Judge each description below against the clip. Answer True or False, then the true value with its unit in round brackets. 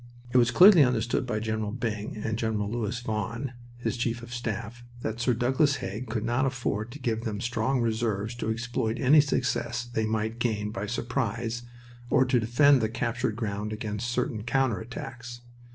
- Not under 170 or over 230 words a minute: True (175 wpm)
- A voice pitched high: False (115 Hz)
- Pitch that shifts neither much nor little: False (2.0 semitones)